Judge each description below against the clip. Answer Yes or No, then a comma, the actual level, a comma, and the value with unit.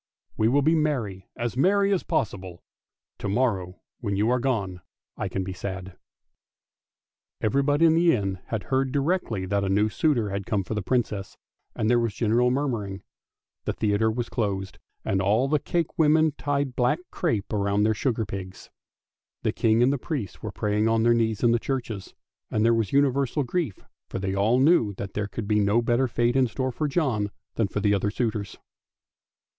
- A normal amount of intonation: Yes, average, 4.8 semitones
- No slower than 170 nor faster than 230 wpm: Yes, average, 190 wpm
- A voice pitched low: Yes, low, 115 Hz